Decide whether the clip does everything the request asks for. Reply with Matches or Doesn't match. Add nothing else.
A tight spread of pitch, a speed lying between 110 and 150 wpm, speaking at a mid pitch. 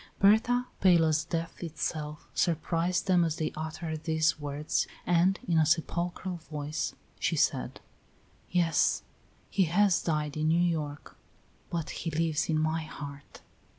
Matches